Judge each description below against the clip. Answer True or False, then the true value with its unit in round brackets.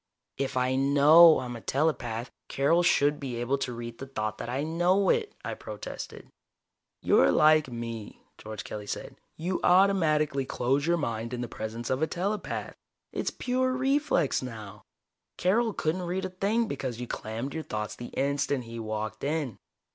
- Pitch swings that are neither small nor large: False (6.4 semitones)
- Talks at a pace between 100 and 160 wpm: False (170 wpm)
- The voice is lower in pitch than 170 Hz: True (140 Hz)